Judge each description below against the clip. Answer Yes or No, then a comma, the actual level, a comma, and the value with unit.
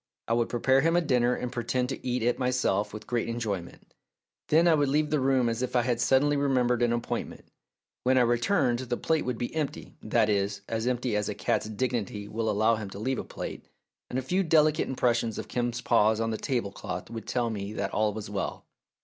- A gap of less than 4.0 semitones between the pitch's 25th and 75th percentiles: Yes, average, 2.9 semitones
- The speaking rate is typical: No, fast, 225 wpm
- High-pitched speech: No, low, 120 Hz